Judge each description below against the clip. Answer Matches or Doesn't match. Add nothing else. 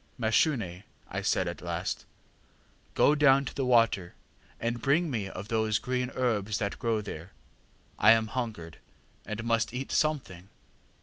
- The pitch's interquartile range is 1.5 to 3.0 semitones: Doesn't match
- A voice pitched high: Doesn't match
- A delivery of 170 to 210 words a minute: Doesn't match